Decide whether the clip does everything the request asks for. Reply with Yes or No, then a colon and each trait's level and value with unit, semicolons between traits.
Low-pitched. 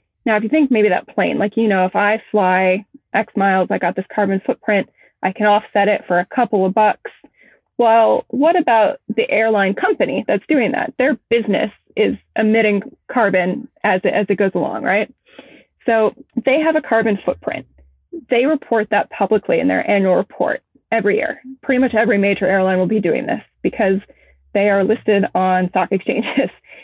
No: high, 215 Hz